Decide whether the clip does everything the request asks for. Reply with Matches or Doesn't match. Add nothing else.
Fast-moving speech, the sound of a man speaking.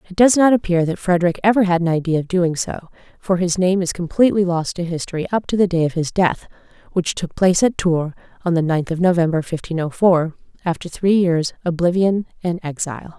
Doesn't match